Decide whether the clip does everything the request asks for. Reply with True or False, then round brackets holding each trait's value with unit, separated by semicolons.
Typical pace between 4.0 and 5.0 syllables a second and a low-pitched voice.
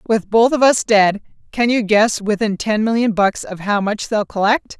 False (4.6 syllables/s; 215 Hz)